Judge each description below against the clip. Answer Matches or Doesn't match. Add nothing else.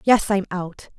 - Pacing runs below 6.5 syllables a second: Matches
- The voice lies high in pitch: Matches